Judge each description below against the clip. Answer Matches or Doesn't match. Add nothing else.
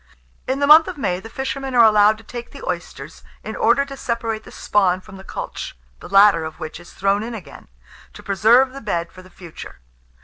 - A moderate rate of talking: Doesn't match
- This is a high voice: Matches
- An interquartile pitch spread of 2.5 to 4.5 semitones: Doesn't match